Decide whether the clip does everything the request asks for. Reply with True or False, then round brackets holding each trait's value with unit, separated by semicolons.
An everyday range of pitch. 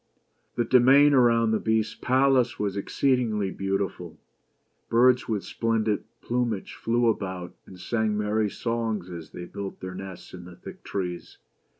True (3.7 semitones)